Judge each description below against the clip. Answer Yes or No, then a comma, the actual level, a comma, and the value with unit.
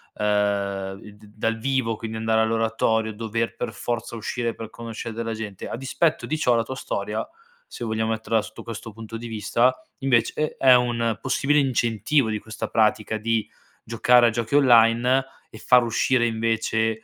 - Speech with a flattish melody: Yes, narrow, 1.4 semitones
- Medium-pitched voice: No, low, 115 Hz